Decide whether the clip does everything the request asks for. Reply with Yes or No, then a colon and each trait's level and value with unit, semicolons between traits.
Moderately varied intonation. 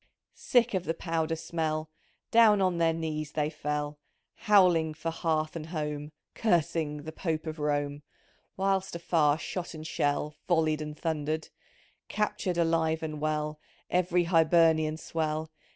No: narrow, 1.8 semitones